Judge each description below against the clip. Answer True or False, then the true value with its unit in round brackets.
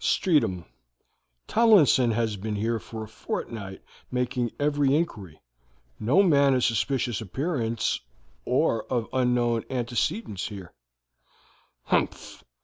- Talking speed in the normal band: False (100 wpm)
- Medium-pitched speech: False (120 Hz)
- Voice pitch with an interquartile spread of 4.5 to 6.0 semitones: False (3.9 semitones)